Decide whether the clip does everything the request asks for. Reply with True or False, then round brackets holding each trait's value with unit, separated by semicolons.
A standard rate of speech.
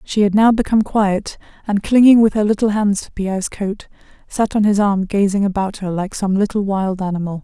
False (210 wpm)